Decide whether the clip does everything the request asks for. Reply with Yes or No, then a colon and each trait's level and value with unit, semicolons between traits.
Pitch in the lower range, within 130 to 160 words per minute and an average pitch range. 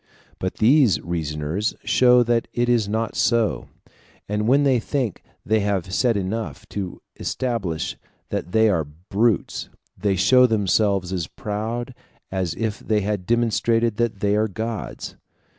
Yes: low, 105 Hz; average, 140 wpm; average, 3.5 semitones